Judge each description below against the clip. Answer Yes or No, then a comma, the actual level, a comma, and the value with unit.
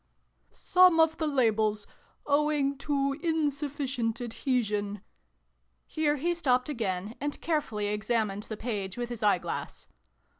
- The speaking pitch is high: Yes, very high, 250 Hz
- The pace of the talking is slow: Yes, slow, 120 wpm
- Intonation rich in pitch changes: Yes, wide, 5.7 semitones